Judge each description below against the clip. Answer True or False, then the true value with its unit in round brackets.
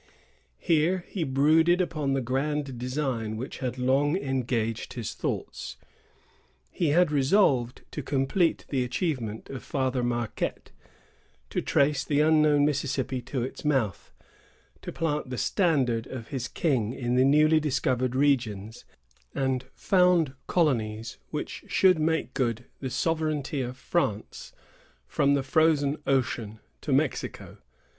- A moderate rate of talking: False (130 wpm)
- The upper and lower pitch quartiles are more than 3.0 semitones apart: True (3.5 semitones)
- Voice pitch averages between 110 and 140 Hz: True (135 Hz)